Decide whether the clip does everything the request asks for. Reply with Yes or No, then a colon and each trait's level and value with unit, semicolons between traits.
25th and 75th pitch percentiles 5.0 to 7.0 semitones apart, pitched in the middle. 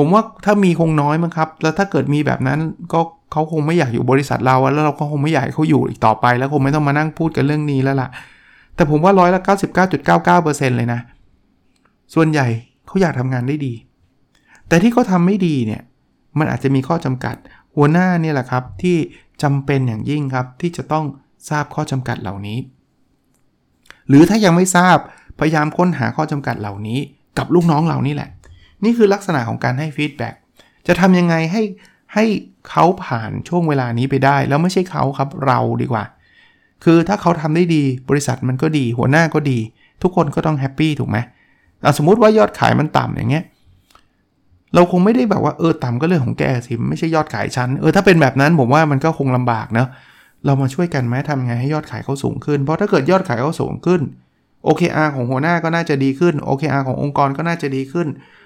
No: average, 4.2 semitones; medium, 150 Hz